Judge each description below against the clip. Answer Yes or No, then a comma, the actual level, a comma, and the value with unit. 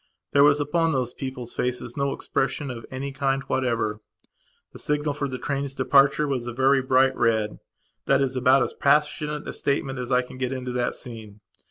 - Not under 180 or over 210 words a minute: Yes, average, 190 wpm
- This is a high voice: No, low, 135 Hz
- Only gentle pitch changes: Yes, narrow, 2.0 semitones